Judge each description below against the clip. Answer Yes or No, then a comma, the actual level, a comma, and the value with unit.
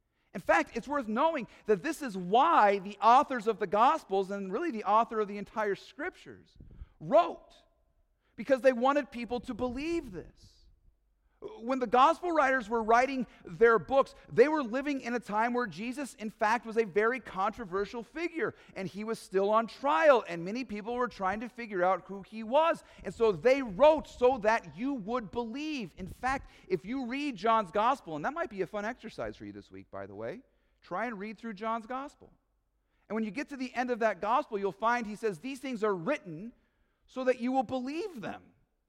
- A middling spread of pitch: Yes, average, 4.1 semitones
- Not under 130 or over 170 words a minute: No, average, 200 wpm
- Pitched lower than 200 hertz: No, high, 235 Hz